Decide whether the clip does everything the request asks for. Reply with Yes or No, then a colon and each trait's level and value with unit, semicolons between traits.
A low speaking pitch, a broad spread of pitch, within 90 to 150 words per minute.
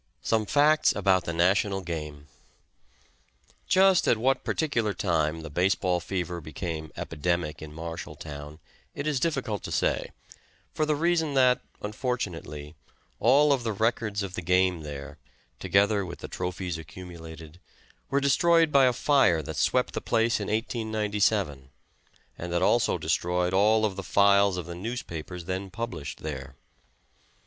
Yes: very low, 95 Hz; wide, 5.9 semitones; average, 145 wpm